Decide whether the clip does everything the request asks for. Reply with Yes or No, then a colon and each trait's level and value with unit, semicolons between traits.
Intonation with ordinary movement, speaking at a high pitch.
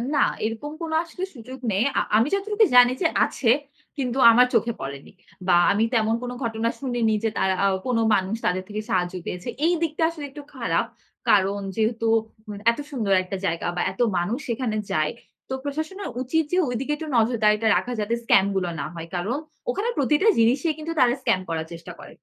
No: wide, 6.1 semitones; high, 230 Hz